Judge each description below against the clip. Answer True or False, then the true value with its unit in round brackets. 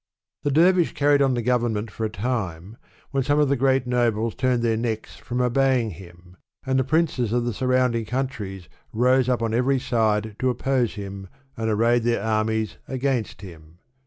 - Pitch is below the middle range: True (120 Hz)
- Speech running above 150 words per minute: True (185 wpm)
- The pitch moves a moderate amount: True (3.3 semitones)